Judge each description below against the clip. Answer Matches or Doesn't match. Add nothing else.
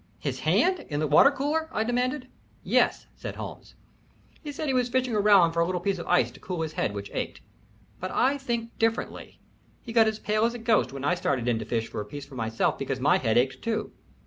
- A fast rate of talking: Matches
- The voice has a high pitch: Matches